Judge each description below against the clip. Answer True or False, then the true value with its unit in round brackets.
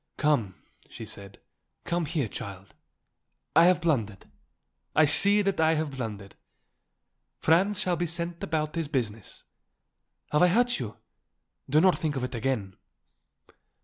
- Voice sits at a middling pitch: True (150 Hz)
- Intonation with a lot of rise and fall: True (7.0 semitones)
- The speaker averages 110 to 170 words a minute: True (140 wpm)